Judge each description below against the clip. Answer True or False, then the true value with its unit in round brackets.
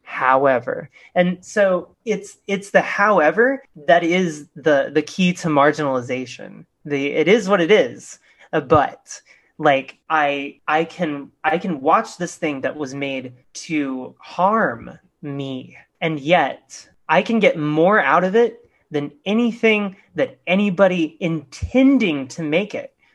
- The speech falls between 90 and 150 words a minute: True (135 wpm)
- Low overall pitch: False (165 Hz)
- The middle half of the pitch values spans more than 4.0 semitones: True (5.4 semitones)